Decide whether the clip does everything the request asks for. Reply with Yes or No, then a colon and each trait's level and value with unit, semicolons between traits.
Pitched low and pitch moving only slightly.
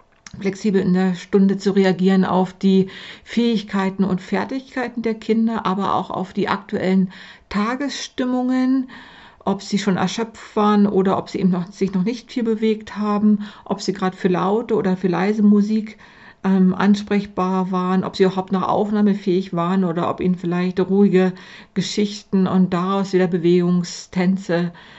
No: high, 195 Hz; narrow, 2.1 semitones